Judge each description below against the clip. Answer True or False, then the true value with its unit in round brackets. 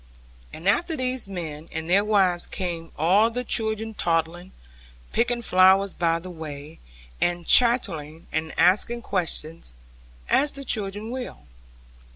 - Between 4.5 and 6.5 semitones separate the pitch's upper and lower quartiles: True (5.2 semitones)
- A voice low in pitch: False (185 Hz)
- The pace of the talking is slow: True (130 wpm)